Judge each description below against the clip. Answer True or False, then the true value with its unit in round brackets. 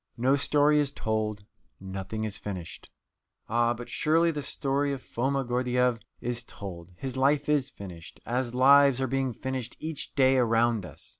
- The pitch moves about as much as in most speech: True (3.8 semitones)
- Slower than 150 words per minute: False (160 wpm)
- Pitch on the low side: True (125 Hz)